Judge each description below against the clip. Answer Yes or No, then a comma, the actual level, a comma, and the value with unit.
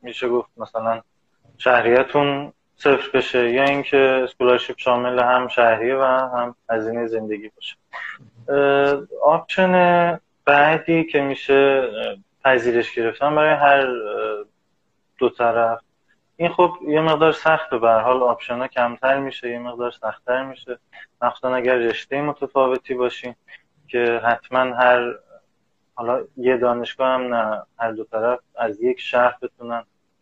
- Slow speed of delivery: No, average, 125 wpm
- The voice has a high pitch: No, low, 125 Hz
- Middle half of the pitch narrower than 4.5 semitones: Yes, average, 2.7 semitones